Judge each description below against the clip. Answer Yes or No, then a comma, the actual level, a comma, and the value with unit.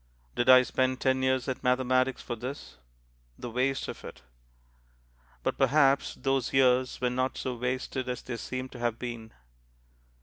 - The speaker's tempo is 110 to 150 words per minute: No, average, 160 wpm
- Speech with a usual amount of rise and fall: No, narrow, 1.0 semitones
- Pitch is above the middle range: No, low, 130 Hz